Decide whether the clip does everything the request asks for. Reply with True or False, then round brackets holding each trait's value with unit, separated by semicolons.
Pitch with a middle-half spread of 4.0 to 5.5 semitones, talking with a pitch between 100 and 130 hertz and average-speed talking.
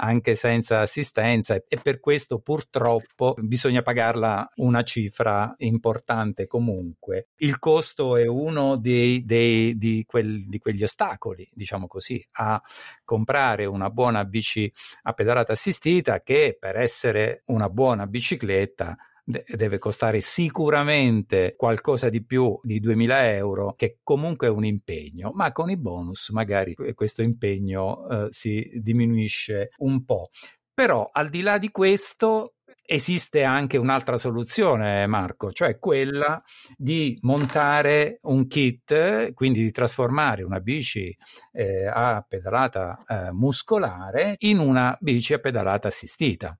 True (4.4 semitones; 120 Hz; 125 wpm)